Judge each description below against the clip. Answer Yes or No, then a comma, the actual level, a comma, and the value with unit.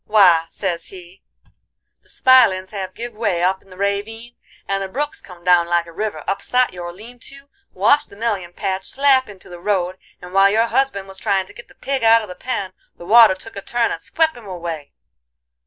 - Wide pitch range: No, average, 4.2 semitones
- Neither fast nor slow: No, fast, 215 wpm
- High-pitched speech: Yes, high, 195 Hz